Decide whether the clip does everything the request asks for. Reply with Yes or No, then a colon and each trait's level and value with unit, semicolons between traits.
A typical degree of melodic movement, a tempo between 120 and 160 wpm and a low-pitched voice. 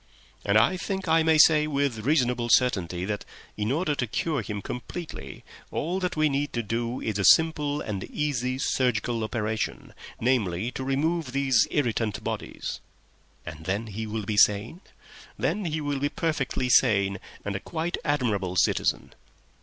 No: wide, 5.9 semitones; average, 155 wpm; low, 125 Hz